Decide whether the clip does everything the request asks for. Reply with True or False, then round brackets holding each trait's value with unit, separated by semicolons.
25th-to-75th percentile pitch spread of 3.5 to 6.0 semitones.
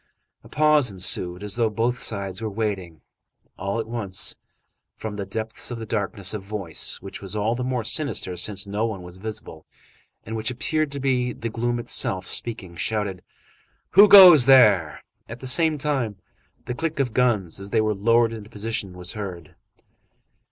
True (3.9 semitones)